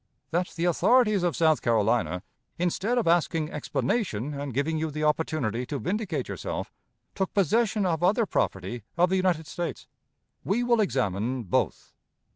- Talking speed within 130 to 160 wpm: Yes, average, 150 wpm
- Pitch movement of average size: No, wide, 6.3 semitones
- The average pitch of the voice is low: No, medium, 160 Hz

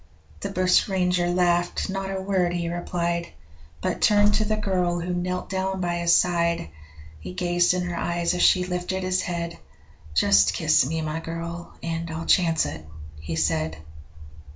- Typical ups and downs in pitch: No, narrow, 1.5 semitones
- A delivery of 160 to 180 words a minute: Yes, average, 165 wpm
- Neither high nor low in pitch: Yes, medium, 175 Hz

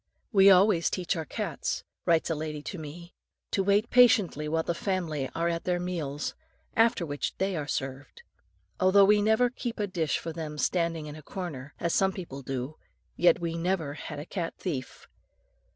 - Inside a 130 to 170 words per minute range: No, average, 185 wpm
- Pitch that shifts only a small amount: No, average, 4.1 semitones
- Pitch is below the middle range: No, medium, 170 Hz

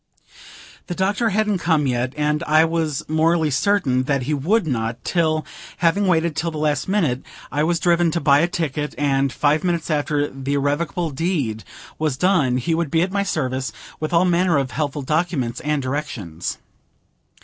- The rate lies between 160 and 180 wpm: Yes, average, 175 wpm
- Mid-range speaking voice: Yes, medium, 155 Hz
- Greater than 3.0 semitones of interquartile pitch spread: Yes, average, 3.8 semitones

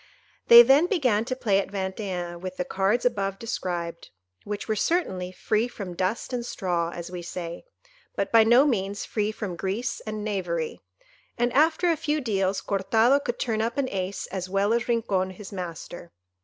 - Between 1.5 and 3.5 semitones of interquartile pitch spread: No, average, 4.3 semitones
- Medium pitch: No, high, 205 Hz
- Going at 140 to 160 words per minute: No, average, 185 wpm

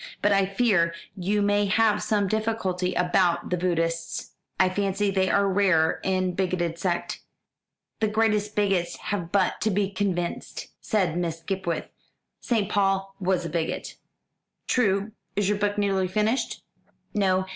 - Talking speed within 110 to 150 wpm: Yes, average, 145 wpm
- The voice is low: No, high, 195 Hz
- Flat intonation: Yes, narrow, 2.3 semitones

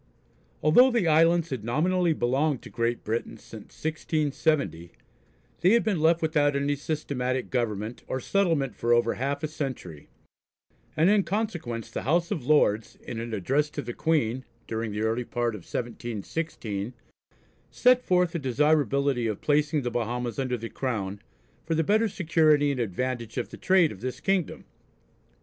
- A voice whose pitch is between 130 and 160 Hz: Yes, low, 135 Hz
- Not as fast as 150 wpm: No, average, 160 wpm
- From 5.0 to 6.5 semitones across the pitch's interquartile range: Yes, average, 5.3 semitones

